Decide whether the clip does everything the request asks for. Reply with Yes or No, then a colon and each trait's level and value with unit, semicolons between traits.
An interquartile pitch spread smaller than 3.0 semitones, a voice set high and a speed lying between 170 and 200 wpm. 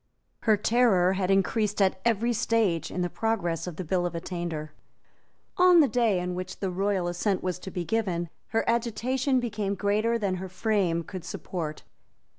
No: average, 4.1 semitones; high, 195 Hz; average, 175 wpm